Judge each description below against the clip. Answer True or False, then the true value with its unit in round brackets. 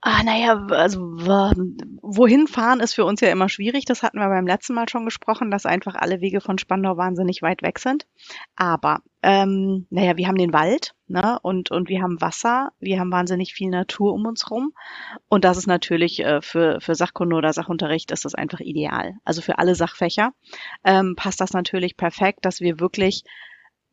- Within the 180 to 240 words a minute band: True (190 wpm)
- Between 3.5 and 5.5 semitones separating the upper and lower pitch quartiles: True (4.0 semitones)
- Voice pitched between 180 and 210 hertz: True (190 Hz)